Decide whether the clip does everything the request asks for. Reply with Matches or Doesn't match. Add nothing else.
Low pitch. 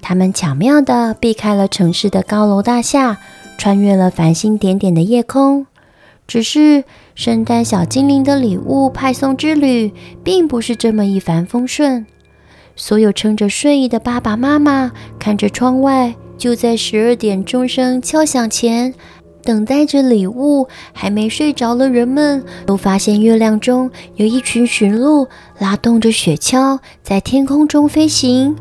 Doesn't match